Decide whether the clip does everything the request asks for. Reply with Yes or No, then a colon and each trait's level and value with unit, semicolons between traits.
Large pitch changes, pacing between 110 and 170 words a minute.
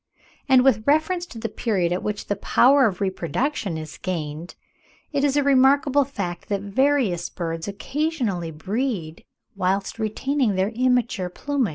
Yes: wide, 7.0 semitones; average, 150 wpm